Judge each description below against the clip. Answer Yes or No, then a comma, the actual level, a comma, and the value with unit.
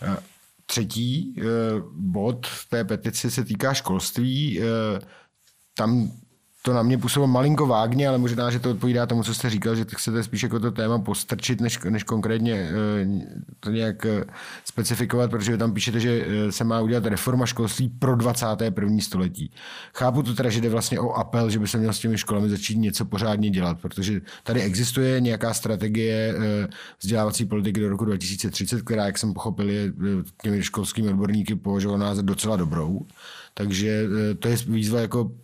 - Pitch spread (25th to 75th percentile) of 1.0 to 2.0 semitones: No, narrow, 2.5 semitones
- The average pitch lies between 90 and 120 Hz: Yes, low, 110 Hz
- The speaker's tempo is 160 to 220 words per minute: Yes, average, 165 wpm